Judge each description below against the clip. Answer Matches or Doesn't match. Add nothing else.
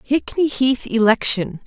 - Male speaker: Doesn't match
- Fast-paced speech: Doesn't match